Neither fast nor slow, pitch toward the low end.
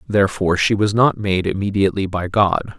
Yes: average, 170 wpm; low, 100 Hz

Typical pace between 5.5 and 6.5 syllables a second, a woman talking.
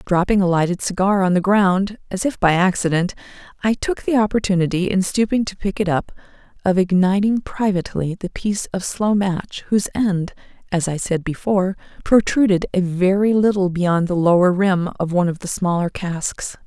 No: 5.2 syllables/s; female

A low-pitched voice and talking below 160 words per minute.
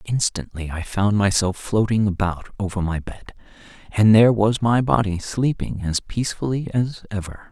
Yes: low, 105 Hz; average, 150 wpm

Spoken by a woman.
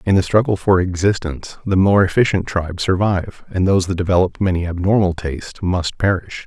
No: male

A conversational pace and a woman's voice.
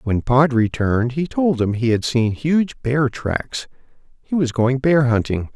No: average, 185 wpm; male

